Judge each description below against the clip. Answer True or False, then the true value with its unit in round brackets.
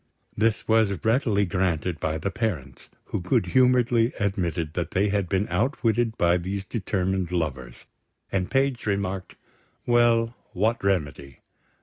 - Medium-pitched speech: False (100 Hz)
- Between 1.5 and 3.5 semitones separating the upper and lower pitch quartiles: False (4.5 semitones)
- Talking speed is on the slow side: True (130 wpm)